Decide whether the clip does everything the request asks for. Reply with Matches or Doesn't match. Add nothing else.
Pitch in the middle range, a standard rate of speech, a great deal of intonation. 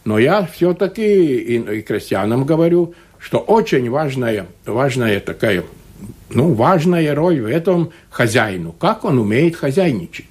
Matches